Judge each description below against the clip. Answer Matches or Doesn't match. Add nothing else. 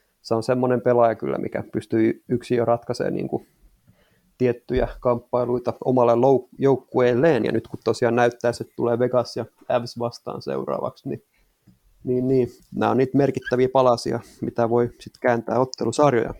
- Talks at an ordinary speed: Matches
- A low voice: Matches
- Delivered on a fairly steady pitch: Matches